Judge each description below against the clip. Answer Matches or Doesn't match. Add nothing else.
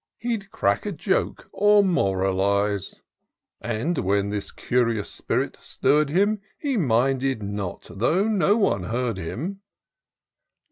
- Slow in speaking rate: Matches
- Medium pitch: Doesn't match